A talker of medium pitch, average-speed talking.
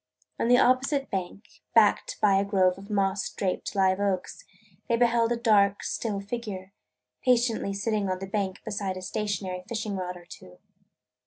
No: high, 200 Hz; average, 165 wpm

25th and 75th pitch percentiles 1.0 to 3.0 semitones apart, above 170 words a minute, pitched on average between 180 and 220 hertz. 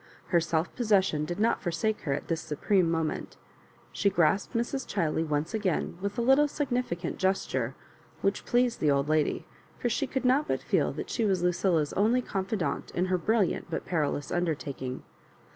No: wide, 5.6 semitones; average, 185 wpm; medium, 185 Hz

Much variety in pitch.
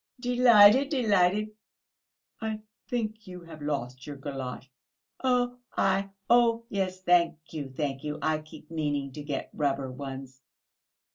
Yes: wide, 7.4 semitones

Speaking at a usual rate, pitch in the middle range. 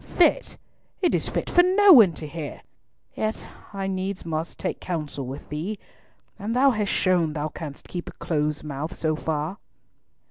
Yes: average, 170 wpm; medium, 170 Hz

